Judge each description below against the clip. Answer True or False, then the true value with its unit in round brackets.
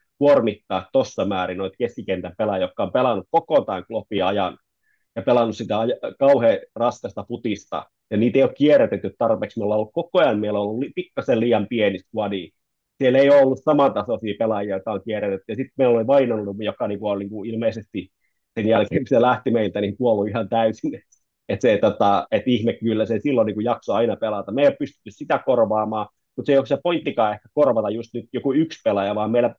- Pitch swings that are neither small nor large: True (4.6 semitones)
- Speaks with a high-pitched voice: False (115 Hz)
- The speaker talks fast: True (200 wpm)